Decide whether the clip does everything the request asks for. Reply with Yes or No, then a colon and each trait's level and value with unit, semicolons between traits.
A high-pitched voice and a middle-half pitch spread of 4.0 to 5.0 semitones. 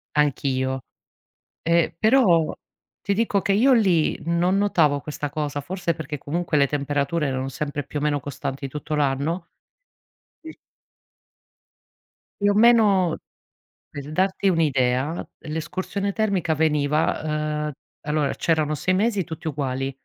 No: medium, 155 Hz; average, 4.4 semitones